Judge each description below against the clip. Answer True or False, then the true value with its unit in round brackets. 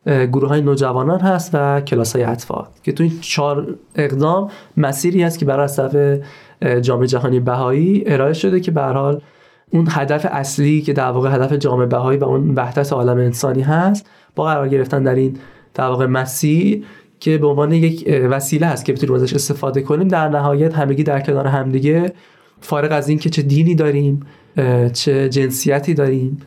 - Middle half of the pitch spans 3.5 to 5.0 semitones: False (2.6 semitones)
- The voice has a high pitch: False (140 Hz)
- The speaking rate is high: True (170 wpm)